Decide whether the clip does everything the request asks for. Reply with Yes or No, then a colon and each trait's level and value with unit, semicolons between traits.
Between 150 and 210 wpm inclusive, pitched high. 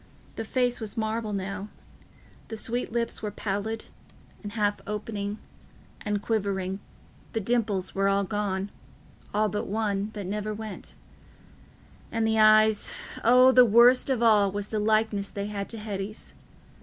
No: average, 140 wpm; high, 210 Hz